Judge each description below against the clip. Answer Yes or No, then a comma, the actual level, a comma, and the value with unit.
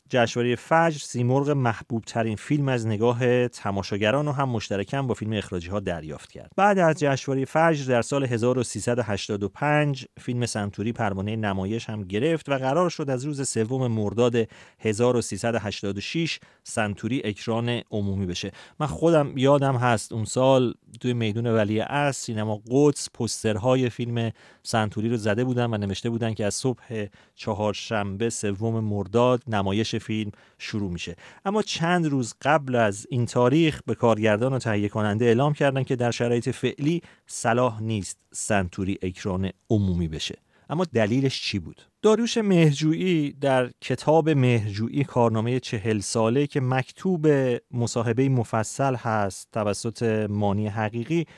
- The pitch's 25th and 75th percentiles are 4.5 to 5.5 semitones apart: No, average, 4.0 semitones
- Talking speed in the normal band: Yes, average, 140 wpm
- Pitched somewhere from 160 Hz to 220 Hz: No, low, 120 Hz